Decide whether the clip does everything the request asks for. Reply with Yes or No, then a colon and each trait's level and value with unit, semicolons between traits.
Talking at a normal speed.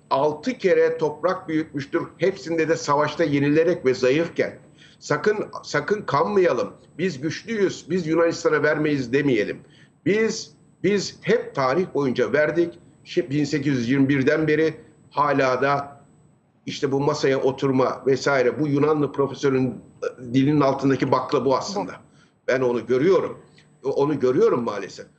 Yes: average, 115 wpm